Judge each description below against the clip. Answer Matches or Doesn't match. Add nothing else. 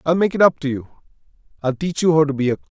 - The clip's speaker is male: Matches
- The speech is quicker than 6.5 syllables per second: Matches